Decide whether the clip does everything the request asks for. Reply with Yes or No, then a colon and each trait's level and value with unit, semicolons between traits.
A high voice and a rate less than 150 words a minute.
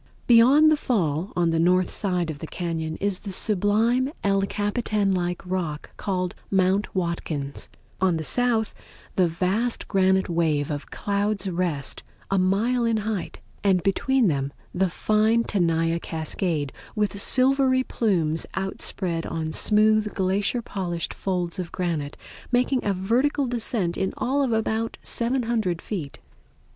Yes: high, 195 Hz; average, 140 wpm